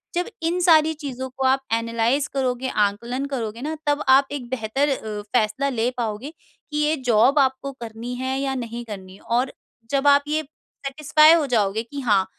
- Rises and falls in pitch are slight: No, average, 3.8 semitones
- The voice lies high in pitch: Yes, very high, 260 Hz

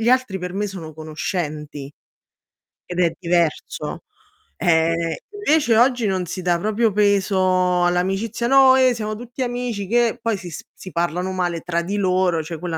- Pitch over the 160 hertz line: Yes, medium, 185 Hz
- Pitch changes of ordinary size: Yes, average, 4.8 semitones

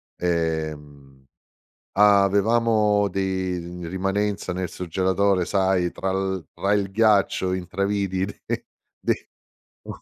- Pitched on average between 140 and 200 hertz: No, very low, 95 Hz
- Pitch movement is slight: Yes, narrow, 2.2 semitones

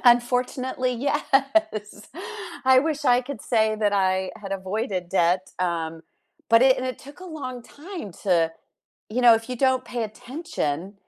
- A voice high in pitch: Yes, high, 240 Hz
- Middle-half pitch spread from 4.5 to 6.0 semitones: Yes, average, 5.1 semitones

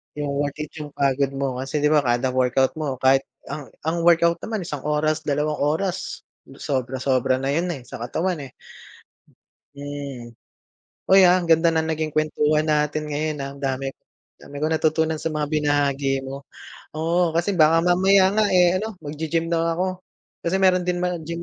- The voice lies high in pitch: No, medium, 155 Hz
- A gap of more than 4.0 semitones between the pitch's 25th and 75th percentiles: No, average, 3.3 semitones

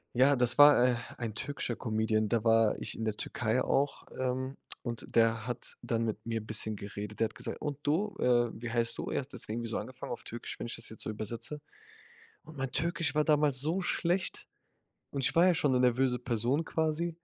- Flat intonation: No, average, 4.2 semitones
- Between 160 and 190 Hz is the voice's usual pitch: No, low, 125 Hz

